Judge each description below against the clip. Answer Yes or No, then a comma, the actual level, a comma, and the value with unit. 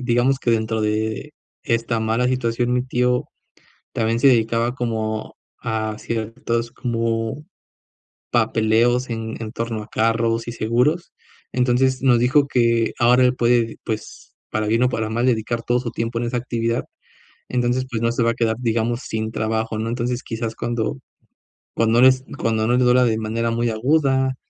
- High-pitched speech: No, low, 115 Hz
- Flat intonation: Yes, narrow, 1.8 semitones